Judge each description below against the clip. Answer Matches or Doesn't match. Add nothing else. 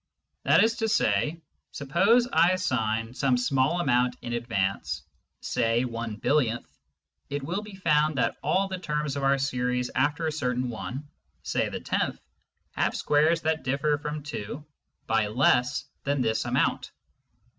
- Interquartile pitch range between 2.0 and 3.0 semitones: Doesn't match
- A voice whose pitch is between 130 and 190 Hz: Matches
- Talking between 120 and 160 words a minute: Matches